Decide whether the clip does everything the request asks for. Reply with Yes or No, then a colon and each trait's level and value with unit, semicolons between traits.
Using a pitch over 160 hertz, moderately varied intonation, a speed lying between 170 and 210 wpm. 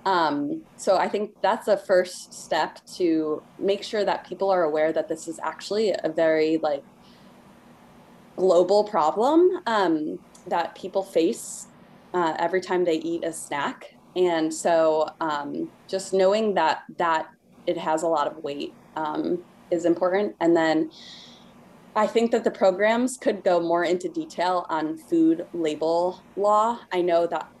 No: medium, 185 Hz; average, 4.3 semitones; average, 150 wpm